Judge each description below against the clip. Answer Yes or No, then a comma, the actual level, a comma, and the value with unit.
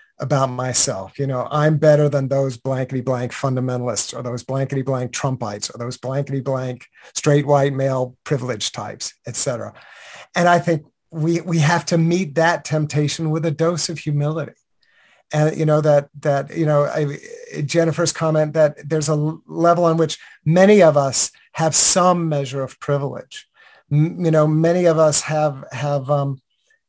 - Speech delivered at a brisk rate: No, average, 165 wpm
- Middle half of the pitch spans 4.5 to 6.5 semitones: No, average, 3.2 semitones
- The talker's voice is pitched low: No, medium, 150 Hz